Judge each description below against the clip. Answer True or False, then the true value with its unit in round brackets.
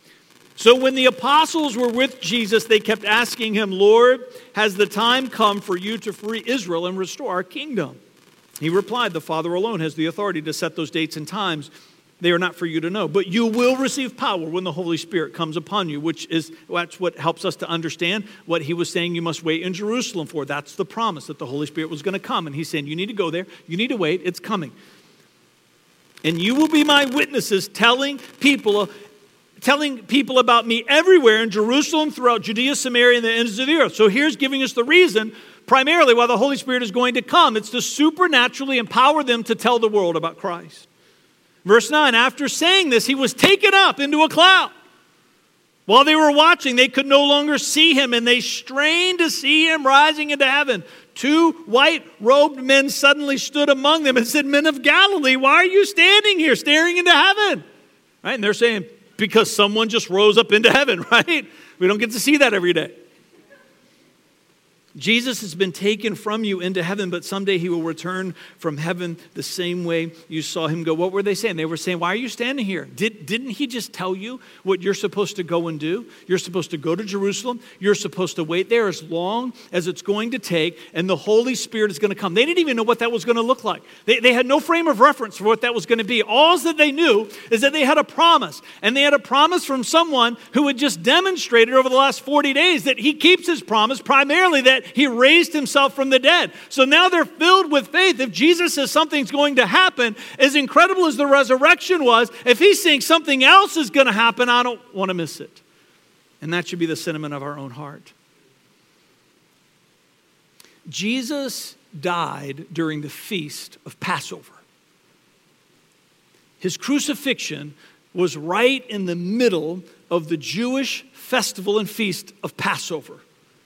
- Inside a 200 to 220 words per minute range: True (205 wpm)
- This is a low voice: False (230 Hz)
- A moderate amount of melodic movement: False (7.2 semitones)